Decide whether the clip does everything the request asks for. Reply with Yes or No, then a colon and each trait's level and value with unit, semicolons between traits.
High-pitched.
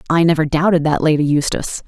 No: medium, 155 Hz